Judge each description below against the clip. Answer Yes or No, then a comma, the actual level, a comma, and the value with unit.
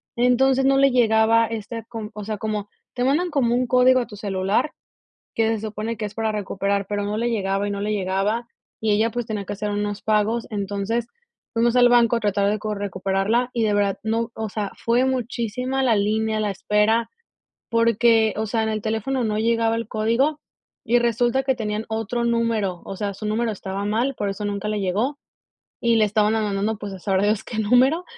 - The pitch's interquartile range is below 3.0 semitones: Yes, narrow, 2.4 semitones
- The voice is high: Yes, high, 220 Hz